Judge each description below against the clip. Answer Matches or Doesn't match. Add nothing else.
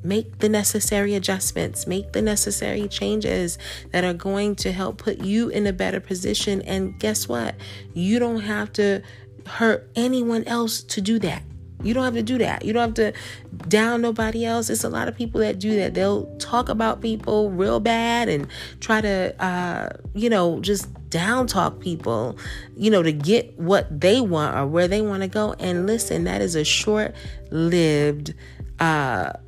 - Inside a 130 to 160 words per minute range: Doesn't match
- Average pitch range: Matches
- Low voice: Doesn't match